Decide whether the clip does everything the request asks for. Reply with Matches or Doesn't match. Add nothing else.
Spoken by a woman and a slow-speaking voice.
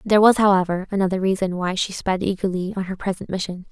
Doesn't match